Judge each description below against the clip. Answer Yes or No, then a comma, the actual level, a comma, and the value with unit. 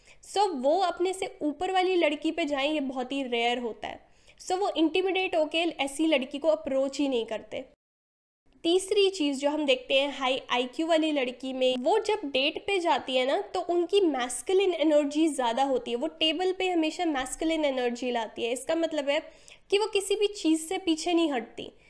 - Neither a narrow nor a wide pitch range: Yes, average, 5.0 semitones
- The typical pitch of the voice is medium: No, very high, 310 Hz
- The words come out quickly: Yes, fast, 200 wpm